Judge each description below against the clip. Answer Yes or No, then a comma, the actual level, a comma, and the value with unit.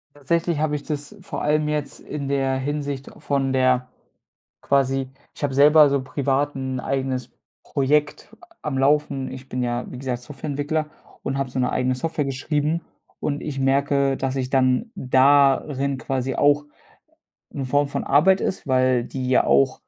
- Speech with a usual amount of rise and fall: No, narrow, 1.9 semitones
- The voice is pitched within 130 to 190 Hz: Yes, low, 135 Hz